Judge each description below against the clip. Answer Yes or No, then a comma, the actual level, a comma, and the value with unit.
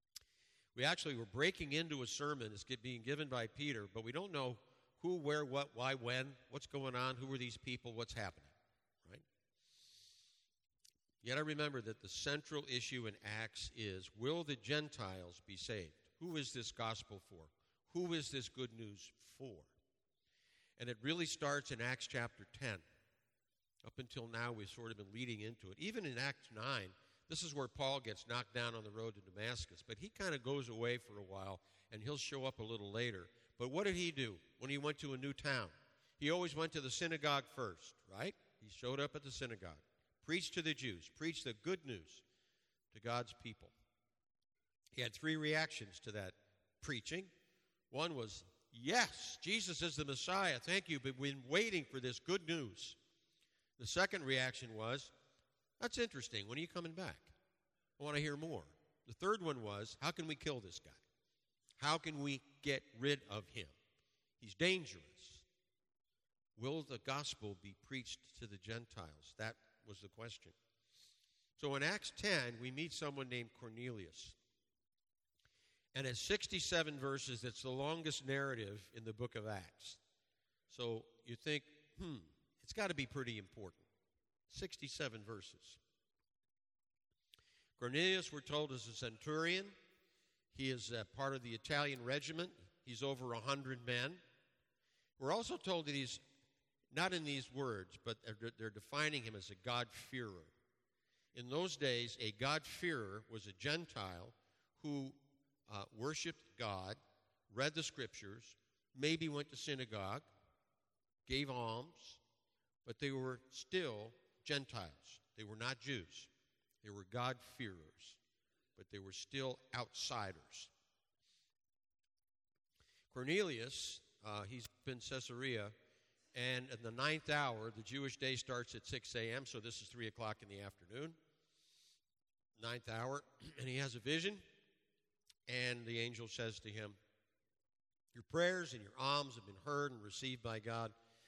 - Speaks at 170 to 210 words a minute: No, average, 160 wpm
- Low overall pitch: Yes, low, 125 Hz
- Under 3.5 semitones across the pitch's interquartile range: No, average, 4.6 semitones